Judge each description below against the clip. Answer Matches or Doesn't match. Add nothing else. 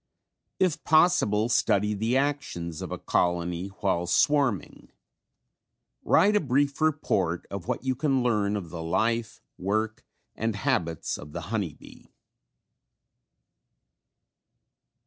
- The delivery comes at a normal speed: Doesn't match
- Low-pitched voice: Matches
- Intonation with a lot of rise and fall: Matches